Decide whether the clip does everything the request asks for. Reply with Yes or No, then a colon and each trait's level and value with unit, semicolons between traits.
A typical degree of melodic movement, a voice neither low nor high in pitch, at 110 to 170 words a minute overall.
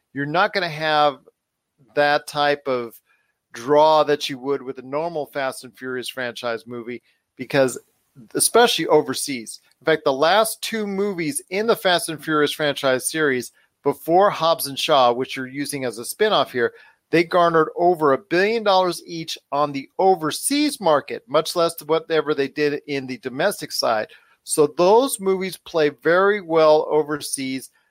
Yes: average, 4.1 semitones; medium, 150 Hz; average, 160 wpm